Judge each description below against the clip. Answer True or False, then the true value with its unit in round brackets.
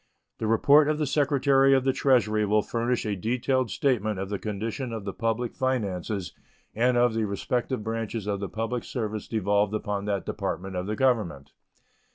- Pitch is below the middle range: True (110 Hz)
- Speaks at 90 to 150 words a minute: False (180 wpm)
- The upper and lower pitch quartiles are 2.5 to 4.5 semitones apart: True (3.6 semitones)